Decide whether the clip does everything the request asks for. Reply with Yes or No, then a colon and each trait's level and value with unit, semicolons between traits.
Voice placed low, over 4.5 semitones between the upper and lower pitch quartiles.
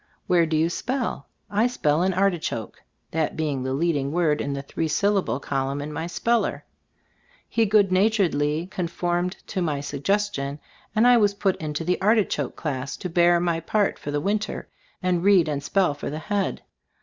No: medium, 170 Hz; average, 5.1 semitones